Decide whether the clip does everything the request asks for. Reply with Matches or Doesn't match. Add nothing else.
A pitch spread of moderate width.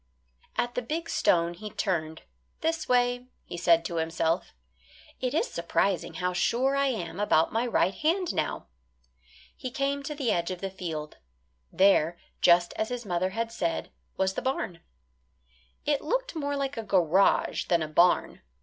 Doesn't match